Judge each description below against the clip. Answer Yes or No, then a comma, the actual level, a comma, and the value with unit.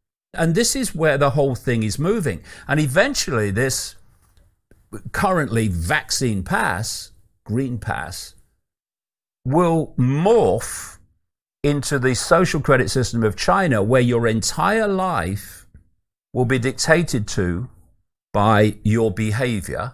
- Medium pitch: No, low, 120 Hz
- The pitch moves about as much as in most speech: No, wide, 6.1 semitones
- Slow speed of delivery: Yes, slow, 110 wpm